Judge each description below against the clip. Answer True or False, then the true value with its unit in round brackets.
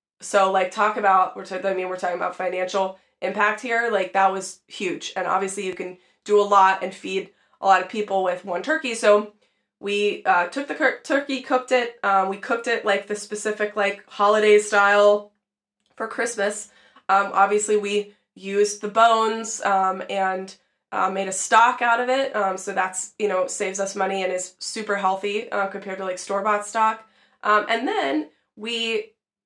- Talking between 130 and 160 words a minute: False (185 wpm)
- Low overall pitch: False (205 Hz)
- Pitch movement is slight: True (2.3 semitones)